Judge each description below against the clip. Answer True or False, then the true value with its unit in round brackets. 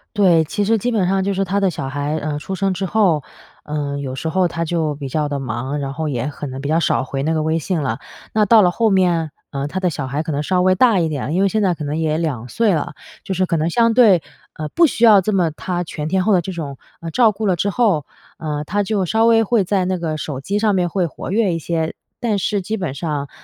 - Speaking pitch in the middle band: True (170 Hz)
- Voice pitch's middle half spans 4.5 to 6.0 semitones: True (4.8 semitones)